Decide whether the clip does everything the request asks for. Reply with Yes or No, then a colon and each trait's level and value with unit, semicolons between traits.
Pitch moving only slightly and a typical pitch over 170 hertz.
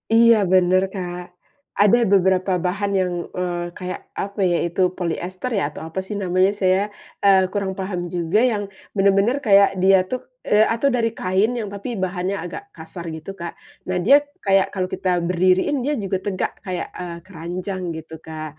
Yes: narrow, 1.9 semitones; medium, 185 Hz